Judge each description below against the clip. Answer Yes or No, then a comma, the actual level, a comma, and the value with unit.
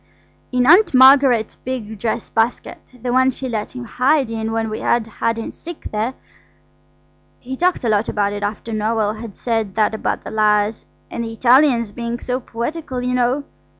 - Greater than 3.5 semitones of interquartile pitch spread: No, average, 2.7 semitones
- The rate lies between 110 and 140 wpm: No, average, 175 wpm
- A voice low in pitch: No, high, 235 Hz